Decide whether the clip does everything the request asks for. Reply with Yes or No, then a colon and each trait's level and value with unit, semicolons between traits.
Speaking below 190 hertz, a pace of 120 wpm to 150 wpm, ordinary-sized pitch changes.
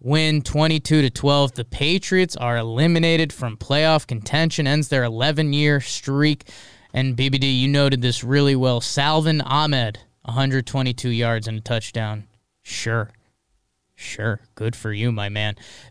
Yes: low, 135 Hz; average, 140 wpm; average, 4.3 semitones